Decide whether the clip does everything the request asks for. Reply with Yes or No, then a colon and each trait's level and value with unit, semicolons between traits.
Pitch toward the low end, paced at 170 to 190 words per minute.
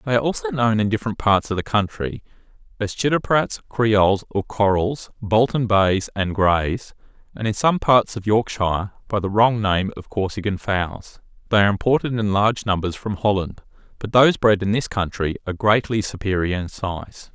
Yes: low, 105 Hz; average, 175 wpm